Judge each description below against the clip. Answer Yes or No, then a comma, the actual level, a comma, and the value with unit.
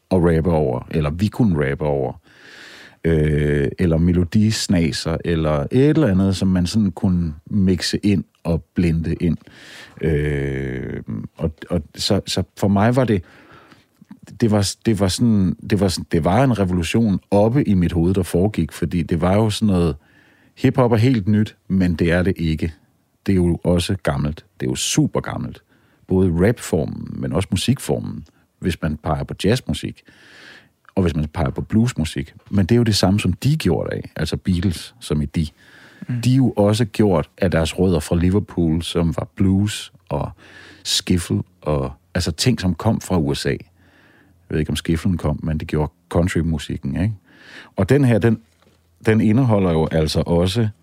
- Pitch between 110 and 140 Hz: No, very low, 90 Hz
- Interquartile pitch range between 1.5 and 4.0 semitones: No, average, 4.5 semitones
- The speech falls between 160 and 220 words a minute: Yes, average, 175 wpm